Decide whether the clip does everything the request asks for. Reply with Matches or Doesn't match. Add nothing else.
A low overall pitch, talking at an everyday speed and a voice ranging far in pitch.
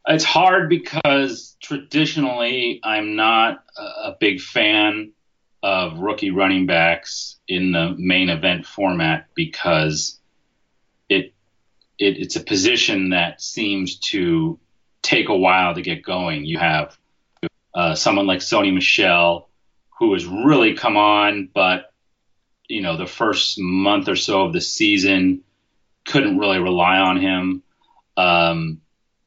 Doesn't match